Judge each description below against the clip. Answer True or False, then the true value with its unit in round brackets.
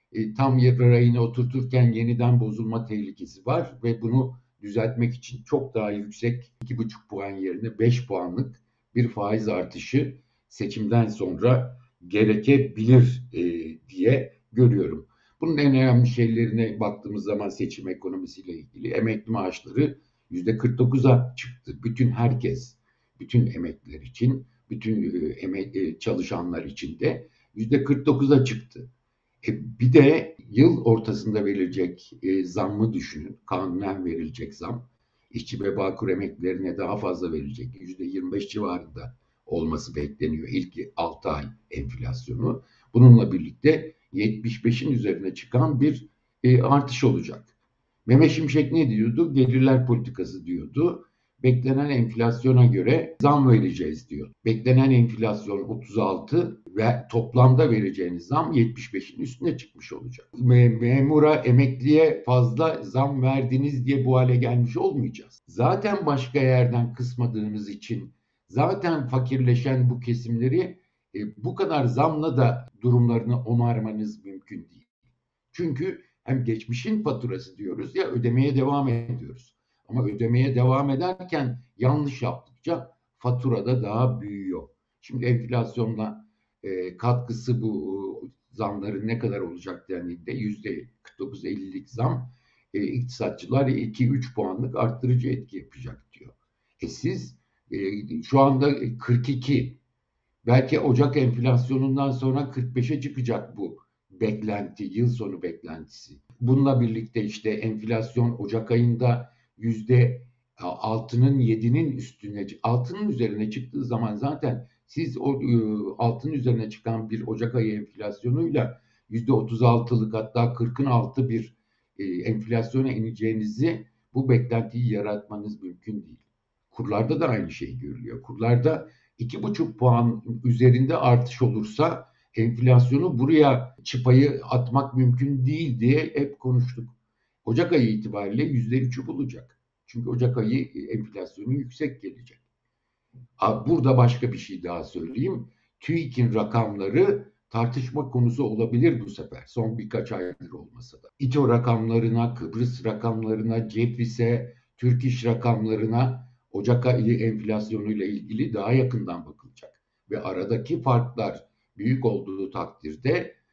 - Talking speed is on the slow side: False (115 wpm)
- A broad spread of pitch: False (2.5 semitones)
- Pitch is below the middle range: True (120 Hz)